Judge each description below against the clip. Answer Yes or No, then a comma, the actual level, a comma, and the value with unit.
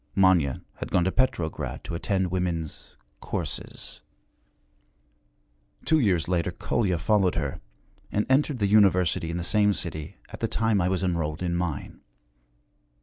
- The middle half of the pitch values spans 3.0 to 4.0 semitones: Yes, average, 3.4 semitones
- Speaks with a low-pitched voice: Yes, very low, 90 Hz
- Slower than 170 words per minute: Yes, average, 145 wpm